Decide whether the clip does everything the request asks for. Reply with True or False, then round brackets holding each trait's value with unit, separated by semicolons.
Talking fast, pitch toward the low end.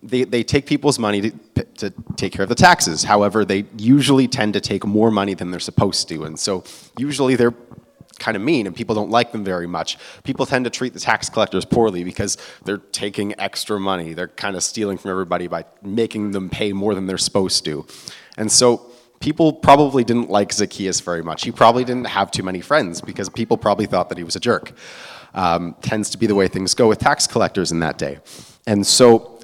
True (220 wpm; 105 Hz)